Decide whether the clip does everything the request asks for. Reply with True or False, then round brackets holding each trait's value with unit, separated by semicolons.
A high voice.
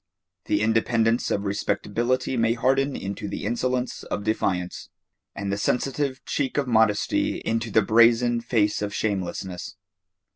False (115 Hz)